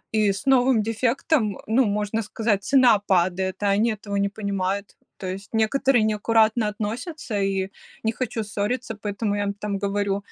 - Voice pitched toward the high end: Yes, high, 210 Hz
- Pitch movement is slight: Yes, narrow, 2.2 semitones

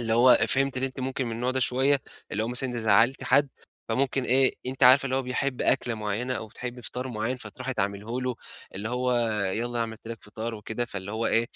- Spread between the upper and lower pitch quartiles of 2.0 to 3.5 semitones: Yes, narrow, 2.5 semitones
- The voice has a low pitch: Yes, low, 125 Hz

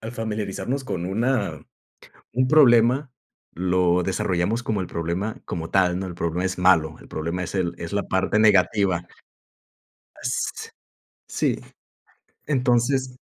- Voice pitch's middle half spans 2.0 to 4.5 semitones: No, average, 5.0 semitones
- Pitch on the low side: Yes, very low, 95 Hz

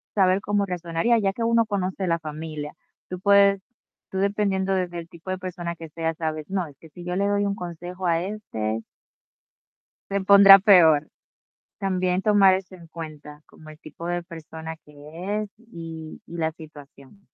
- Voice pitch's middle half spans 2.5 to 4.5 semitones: Yes, average, 3.4 semitones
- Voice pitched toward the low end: No, medium, 180 Hz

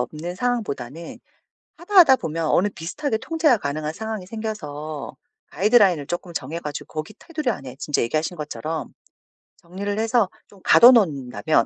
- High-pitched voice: No, medium, 175 Hz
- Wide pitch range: Yes, wide, 6.6 semitones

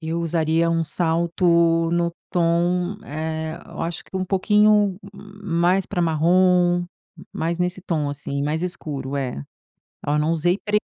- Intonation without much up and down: Yes, narrow, 2.2 semitones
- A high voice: No, medium, 170 Hz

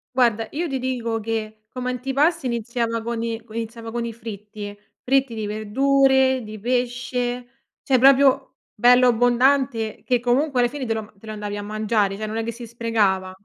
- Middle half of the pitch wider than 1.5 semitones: Yes, average, 2.8 semitones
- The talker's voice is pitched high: Yes, high, 235 Hz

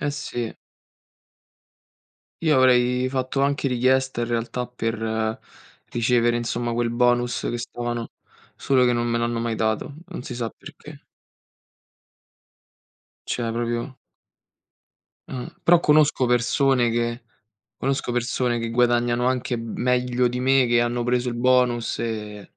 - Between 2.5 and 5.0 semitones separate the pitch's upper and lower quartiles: No, narrow, 1.3 semitones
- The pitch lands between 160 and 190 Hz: No, low, 120 Hz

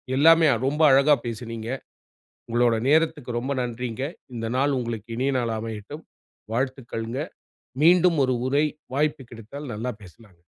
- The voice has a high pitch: No, low, 125 Hz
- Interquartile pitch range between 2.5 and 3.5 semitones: No, average, 3.9 semitones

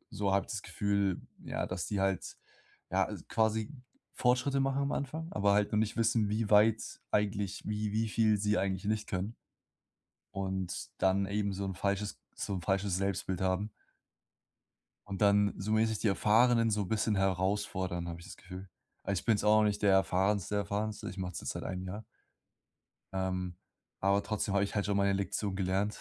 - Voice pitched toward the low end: Yes, low, 100 Hz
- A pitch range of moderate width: No, narrow, 1.9 semitones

